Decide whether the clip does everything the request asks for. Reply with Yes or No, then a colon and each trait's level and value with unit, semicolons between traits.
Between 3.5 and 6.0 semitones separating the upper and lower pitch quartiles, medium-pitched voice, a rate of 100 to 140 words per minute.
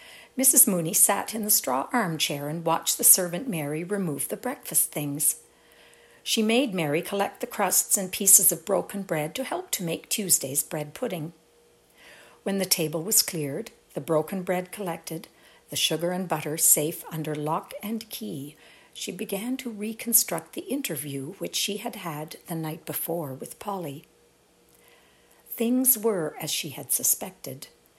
No: wide, 5.6 semitones; medium, 175 Hz; average, 155 wpm